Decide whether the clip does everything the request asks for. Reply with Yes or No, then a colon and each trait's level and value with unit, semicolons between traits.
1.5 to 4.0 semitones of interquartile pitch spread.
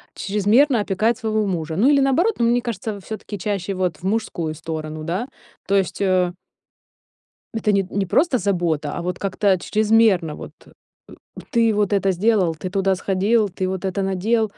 Yes: average, 3.4 semitones